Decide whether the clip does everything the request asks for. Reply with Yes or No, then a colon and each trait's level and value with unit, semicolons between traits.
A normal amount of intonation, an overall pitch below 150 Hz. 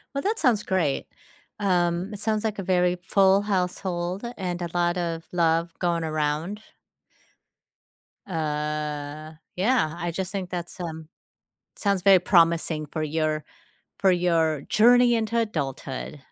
No: average, 3.6 semitones; medium, 175 Hz